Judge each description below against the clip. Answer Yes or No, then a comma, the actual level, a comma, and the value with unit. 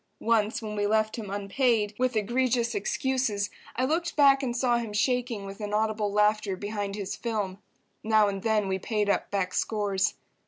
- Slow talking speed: No, average, 170 wpm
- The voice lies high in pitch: Yes, high, 215 Hz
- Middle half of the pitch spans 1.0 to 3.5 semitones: Yes, average, 2.8 semitones